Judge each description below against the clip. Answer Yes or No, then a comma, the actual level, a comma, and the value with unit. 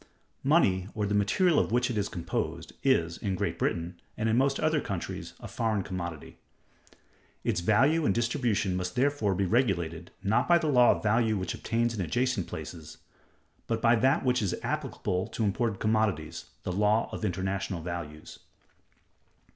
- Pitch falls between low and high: No, low, 105 Hz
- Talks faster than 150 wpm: Yes, average, 165 wpm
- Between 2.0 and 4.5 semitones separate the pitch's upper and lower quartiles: No, average, 4.9 semitones